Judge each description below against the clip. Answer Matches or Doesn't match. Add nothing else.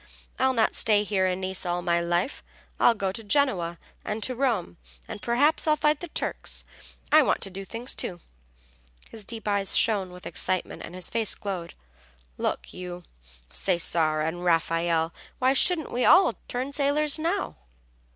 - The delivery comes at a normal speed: Matches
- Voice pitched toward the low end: Doesn't match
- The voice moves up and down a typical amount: Doesn't match